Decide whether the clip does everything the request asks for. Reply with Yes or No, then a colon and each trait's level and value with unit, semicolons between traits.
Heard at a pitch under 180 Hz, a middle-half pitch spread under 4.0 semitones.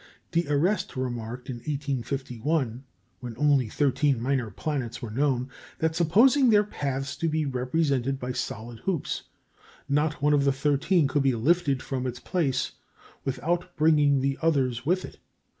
Yes: medium, 140 Hz; average, 3.6 semitones